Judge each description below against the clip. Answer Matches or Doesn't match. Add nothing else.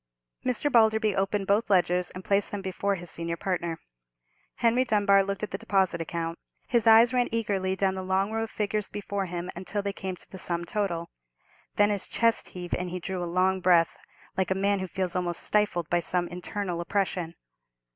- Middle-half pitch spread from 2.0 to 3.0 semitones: Matches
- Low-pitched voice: Doesn't match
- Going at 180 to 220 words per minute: Matches